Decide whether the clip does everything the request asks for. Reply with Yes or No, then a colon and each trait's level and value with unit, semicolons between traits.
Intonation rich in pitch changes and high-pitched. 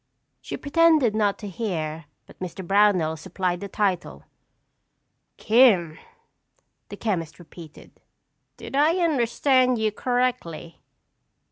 Yes: wide, 6.5 semitones; high, 205 Hz